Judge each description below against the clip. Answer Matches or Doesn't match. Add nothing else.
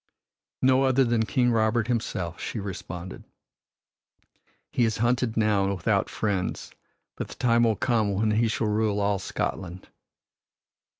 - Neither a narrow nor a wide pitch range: Matches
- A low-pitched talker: Matches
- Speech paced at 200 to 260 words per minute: Doesn't match